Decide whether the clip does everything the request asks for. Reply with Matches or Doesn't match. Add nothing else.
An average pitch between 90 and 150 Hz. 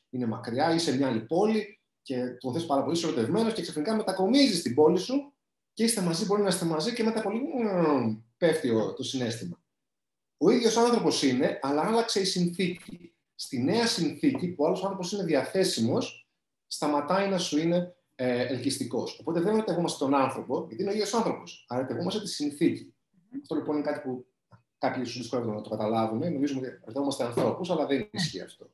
Doesn't match